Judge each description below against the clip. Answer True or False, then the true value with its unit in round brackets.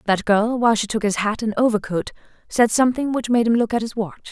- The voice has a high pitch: True (225 Hz)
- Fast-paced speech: True (250 wpm)